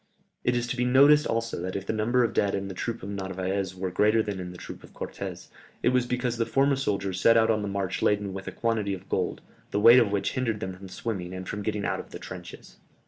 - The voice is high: No, low, 105 Hz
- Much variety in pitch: No, average, 3.5 semitones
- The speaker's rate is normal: No, fast, 260 wpm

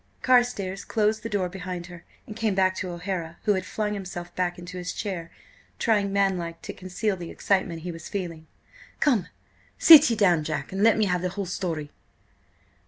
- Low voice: No, medium, 185 Hz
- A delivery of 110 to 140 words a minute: No, average, 185 wpm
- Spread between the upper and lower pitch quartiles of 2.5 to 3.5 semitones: Yes, average, 3.0 semitones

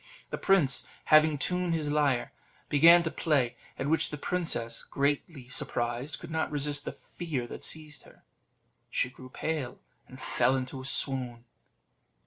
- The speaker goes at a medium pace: Yes, average, 150 wpm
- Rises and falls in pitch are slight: No, average, 3.7 semitones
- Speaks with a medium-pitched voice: Yes, medium, 145 Hz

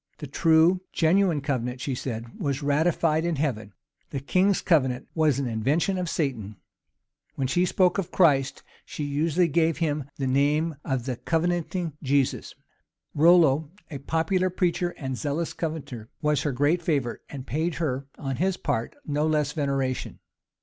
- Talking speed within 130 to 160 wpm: Yes, average, 155 wpm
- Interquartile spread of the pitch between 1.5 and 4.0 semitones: Yes, average, 3.7 semitones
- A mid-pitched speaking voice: Yes, medium, 150 Hz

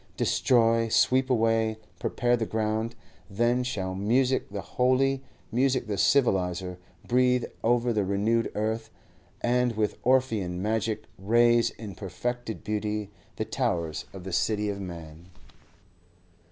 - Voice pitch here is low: Yes, low, 110 Hz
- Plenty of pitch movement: No, average, 3.5 semitones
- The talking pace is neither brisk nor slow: No, slow, 125 wpm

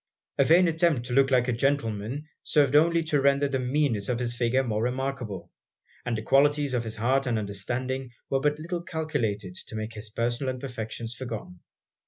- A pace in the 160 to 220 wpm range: Yes, average, 185 wpm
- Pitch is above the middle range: No, low, 130 Hz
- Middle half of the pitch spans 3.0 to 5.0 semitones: Yes, average, 3.8 semitones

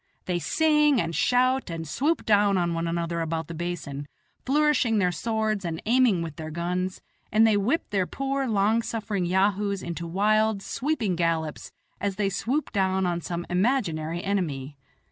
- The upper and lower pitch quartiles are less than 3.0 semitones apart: No, average, 4.8 semitones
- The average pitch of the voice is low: No, high, 195 Hz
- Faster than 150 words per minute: Yes, average, 165 wpm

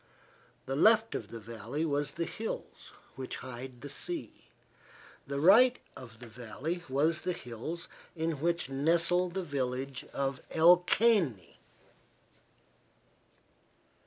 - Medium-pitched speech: Yes, medium, 145 Hz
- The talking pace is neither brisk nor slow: No, slow, 120 wpm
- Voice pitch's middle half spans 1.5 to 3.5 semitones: No, average, 5.2 semitones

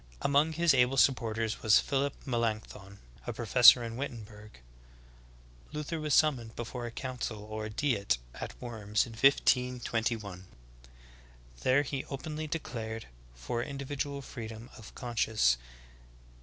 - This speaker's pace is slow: Yes, slow, 120 wpm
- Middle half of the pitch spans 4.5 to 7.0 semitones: No, average, 3.9 semitones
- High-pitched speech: No, low, 120 Hz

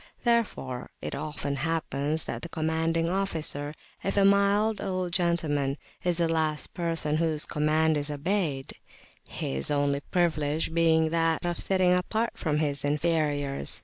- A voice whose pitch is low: No, medium, 160 Hz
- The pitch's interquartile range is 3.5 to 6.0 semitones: No, average, 3.0 semitones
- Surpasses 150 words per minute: No, average, 145 wpm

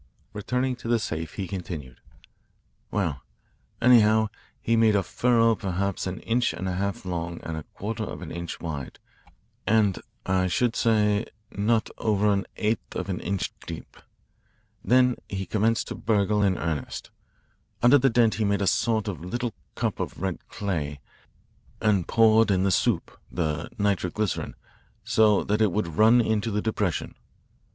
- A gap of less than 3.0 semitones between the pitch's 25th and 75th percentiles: No, average, 3.5 semitones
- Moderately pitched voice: No, low, 105 Hz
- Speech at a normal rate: Yes, average, 160 wpm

